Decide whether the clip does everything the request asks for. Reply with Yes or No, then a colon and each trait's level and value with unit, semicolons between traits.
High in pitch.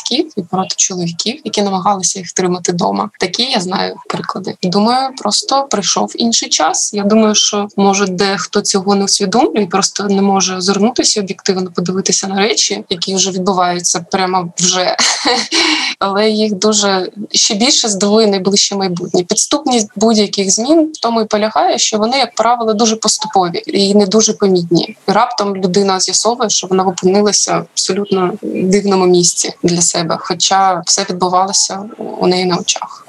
Yes: high, 200 Hz